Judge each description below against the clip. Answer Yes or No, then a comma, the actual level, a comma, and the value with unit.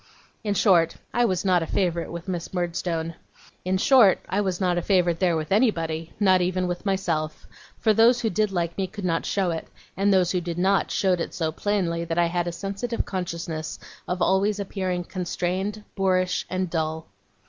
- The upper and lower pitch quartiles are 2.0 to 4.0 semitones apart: Yes, narrow, 2.5 semitones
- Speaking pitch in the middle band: Yes, medium, 180 Hz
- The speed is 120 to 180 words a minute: No, average, 190 wpm